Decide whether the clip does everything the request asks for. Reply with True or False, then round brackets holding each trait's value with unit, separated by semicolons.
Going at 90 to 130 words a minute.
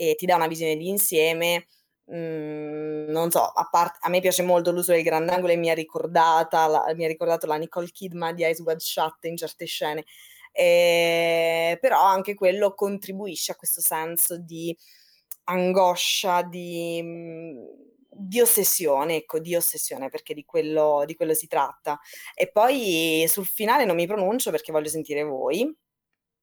False (155 wpm)